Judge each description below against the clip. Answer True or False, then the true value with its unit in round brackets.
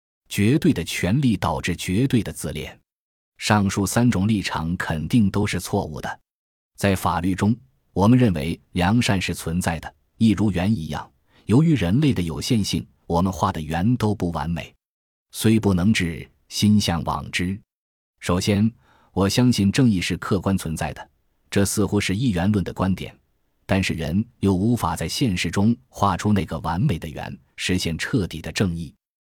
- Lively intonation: False (4.0 semitones)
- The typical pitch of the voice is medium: False (95 Hz)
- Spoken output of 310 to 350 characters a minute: False (240 characters per minute)